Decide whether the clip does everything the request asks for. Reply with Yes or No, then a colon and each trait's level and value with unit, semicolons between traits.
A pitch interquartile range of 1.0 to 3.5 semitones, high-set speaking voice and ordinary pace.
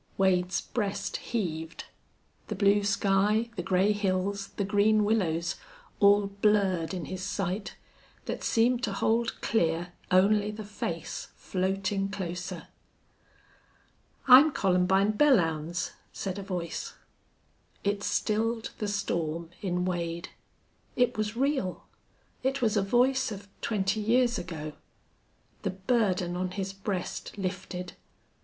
No: average, 2.8 semitones; high, 195 Hz; slow, 120 wpm